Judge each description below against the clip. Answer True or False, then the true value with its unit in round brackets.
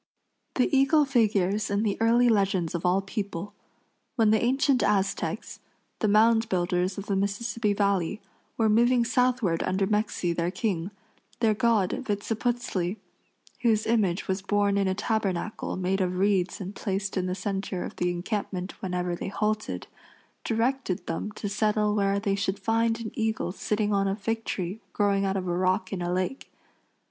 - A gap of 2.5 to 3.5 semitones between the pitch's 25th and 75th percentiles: True (3.0 semitones)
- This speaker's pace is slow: False (165 wpm)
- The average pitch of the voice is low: False (200 Hz)